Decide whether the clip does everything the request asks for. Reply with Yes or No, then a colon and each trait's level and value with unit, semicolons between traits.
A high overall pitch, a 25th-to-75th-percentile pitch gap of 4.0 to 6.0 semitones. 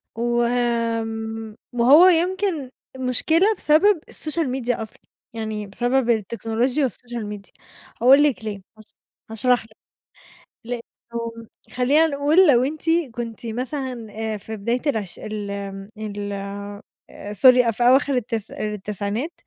No: high, 235 Hz; average, 3.5 semitones